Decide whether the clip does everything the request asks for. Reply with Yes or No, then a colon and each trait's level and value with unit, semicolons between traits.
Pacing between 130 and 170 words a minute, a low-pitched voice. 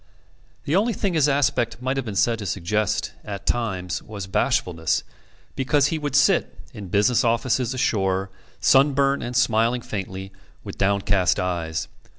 Yes: average, 150 wpm; low, 115 Hz